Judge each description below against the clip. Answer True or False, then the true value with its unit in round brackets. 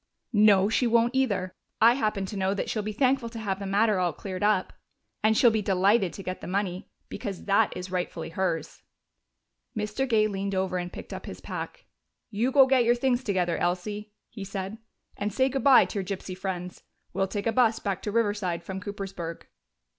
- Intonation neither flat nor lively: True (3.2 semitones)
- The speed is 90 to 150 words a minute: False (200 wpm)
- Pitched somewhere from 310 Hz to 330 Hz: False (200 Hz)